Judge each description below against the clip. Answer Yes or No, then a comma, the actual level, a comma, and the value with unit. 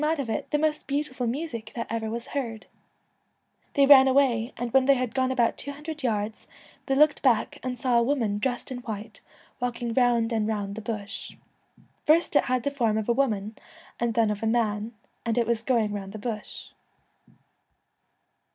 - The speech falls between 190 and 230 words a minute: Yes, average, 195 wpm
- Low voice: No, high, 235 Hz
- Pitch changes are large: No, average, 3.2 semitones